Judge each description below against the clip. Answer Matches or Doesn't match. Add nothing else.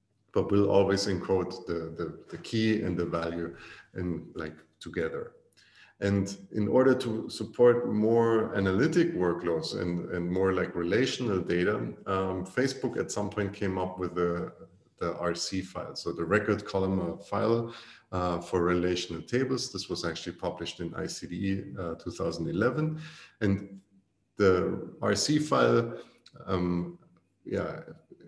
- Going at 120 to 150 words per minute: Matches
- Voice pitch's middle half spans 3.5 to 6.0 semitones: Matches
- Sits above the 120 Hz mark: Doesn't match